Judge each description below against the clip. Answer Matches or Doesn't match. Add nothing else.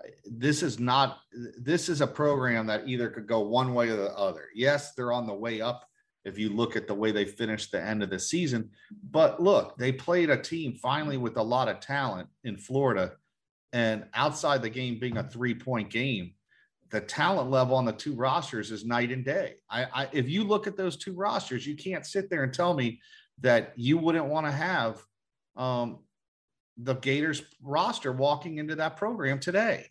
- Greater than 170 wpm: Matches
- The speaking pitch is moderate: Doesn't match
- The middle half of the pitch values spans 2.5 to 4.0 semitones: Doesn't match